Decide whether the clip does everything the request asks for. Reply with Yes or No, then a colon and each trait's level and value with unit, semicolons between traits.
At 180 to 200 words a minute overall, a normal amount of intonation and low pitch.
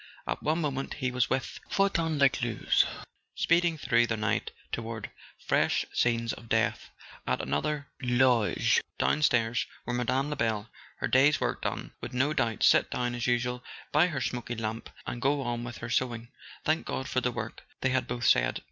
Yes: average, 185 wpm; average, 3.0 semitones; low, 125 Hz